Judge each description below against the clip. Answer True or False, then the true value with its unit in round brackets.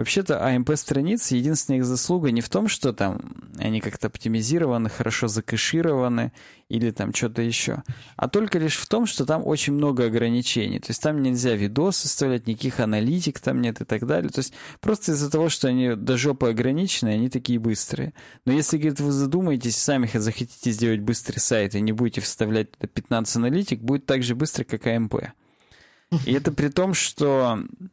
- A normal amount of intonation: True (4.5 semitones)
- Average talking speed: False (175 wpm)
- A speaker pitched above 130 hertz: False (125 Hz)